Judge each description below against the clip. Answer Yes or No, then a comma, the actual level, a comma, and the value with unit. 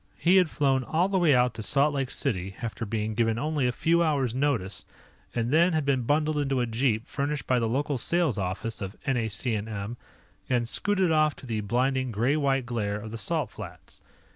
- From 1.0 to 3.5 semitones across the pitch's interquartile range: No, average, 4.7 semitones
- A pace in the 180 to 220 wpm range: Yes, average, 200 wpm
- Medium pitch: No, low, 130 Hz